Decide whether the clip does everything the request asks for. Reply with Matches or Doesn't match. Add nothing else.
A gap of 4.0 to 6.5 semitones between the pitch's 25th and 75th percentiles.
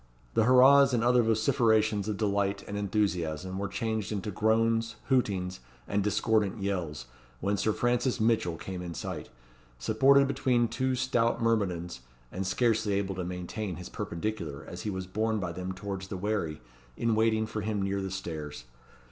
Doesn't match